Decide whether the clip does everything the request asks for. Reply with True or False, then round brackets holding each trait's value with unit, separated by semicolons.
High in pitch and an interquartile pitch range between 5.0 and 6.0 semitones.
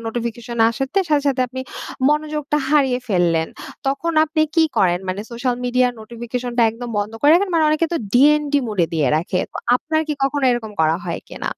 True (250 Hz; 5.3 semitones)